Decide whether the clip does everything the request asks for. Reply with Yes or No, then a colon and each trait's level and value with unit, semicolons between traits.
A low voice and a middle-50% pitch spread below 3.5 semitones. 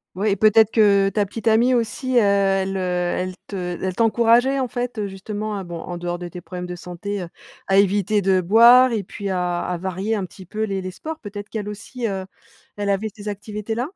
No: high, 205 Hz; average, 2.9 semitones